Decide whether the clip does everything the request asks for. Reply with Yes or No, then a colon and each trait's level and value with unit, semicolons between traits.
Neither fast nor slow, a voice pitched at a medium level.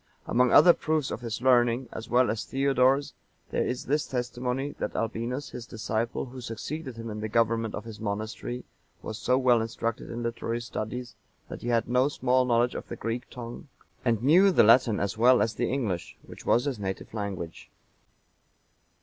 No: average, 185 wpm; low, 120 Hz